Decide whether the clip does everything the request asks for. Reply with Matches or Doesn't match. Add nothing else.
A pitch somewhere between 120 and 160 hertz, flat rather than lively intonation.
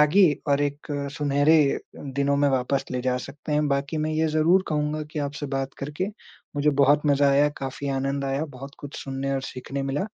Matches